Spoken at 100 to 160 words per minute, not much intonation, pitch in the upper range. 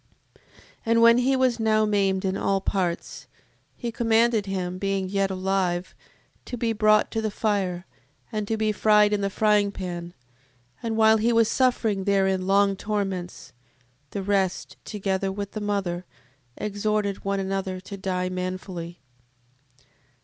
Yes: average, 150 wpm; narrow, 2.2 semitones; high, 200 Hz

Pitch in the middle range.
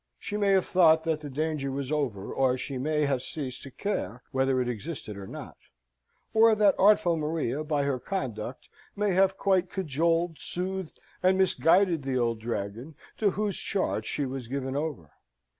Yes: medium, 150 Hz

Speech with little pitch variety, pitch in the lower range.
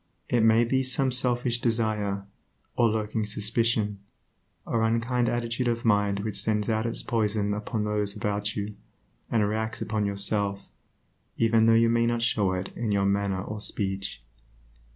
Yes: narrow, 2.2 semitones; low, 110 Hz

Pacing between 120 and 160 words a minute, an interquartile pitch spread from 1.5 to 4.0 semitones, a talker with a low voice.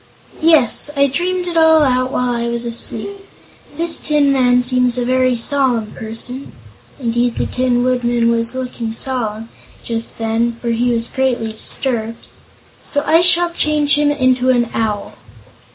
No: average, 155 wpm; average, 3.3 semitones; very high, 250 Hz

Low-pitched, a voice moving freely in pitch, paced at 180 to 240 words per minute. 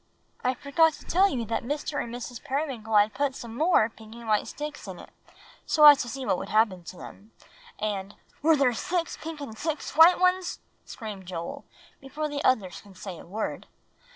No: high, 245 Hz; wide, 5.9 semitones; fast, 205 wpm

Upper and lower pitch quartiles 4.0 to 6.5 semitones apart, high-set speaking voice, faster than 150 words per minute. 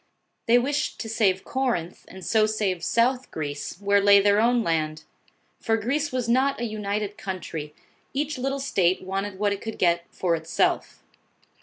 Yes: average, 4.6 semitones; high, 205 Hz; average, 165 wpm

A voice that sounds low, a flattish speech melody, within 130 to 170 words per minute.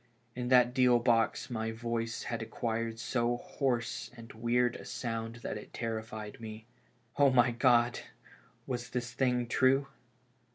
Yes: low, 120 Hz; narrow, 1.4 semitones; average, 140 wpm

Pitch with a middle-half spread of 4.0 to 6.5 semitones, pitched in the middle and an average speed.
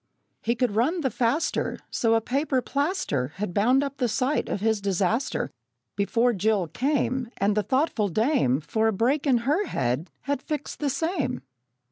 No: average, 5.3 semitones; high, 240 Hz; average, 170 wpm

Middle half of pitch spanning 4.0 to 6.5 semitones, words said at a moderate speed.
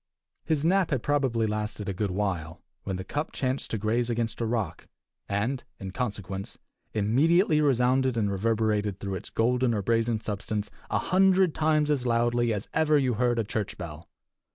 Yes: average, 4.3 semitones; average, 175 wpm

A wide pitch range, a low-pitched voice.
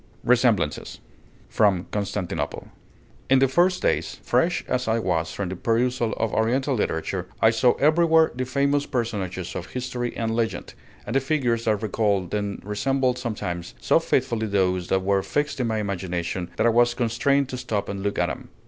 No: average, 4.5 semitones; low, 115 Hz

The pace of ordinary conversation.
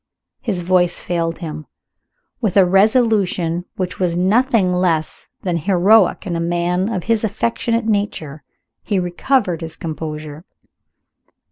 No: slow, 125 wpm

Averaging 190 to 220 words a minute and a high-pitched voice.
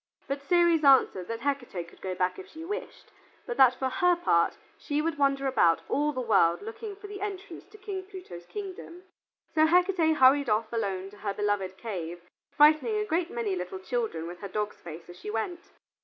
Yes: average, 200 wpm; very high, 270 Hz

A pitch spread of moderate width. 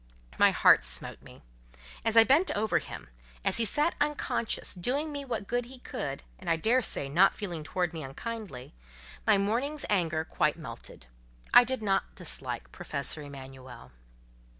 No: wide, 8.2 semitones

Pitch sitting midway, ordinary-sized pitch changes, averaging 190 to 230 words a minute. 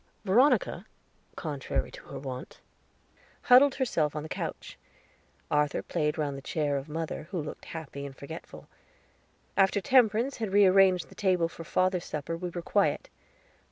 No: medium, 165 Hz; average, 4.7 semitones; average, 150 wpm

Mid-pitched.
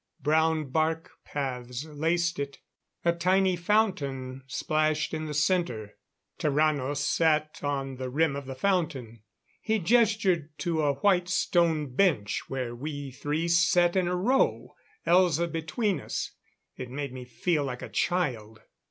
Yes: medium, 155 Hz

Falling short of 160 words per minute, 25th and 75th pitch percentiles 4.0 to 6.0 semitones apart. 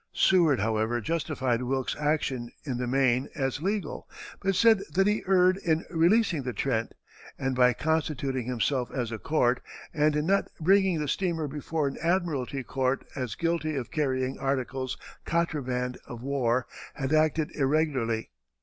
Yes: average, 150 wpm; average, 4.4 semitones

